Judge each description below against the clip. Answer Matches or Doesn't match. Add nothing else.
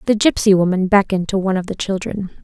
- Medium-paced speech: Doesn't match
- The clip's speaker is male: Doesn't match